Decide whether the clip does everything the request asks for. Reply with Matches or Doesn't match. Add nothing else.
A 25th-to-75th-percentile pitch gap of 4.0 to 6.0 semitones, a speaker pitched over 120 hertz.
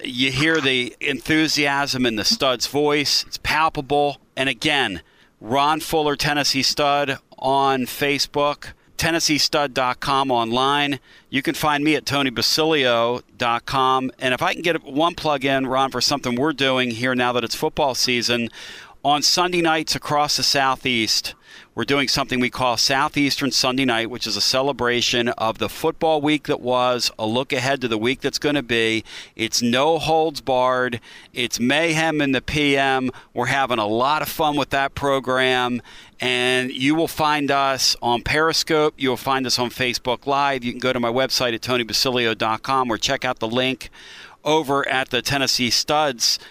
Doesn't match